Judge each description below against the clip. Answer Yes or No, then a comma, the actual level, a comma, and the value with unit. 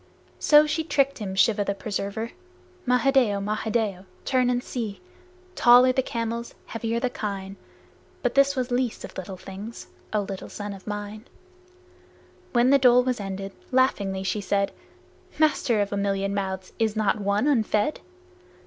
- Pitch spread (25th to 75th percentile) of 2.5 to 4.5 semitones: Yes, average, 3.9 semitones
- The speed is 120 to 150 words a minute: No, average, 160 wpm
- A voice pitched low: No, high, 215 Hz